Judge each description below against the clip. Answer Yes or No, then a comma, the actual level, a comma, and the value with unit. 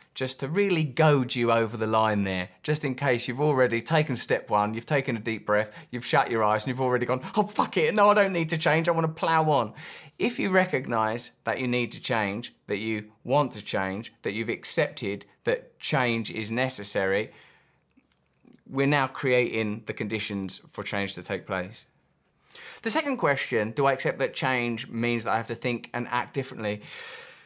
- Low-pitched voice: Yes, low, 120 Hz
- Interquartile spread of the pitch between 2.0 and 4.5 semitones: No, average, 4.9 semitones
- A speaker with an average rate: Yes, average, 195 wpm